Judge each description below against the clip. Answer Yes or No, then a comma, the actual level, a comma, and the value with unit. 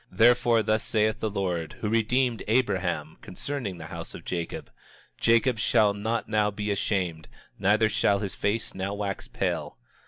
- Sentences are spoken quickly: No, average, 160 wpm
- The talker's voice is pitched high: No, low, 105 Hz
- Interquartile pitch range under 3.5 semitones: Yes, average, 2.7 semitones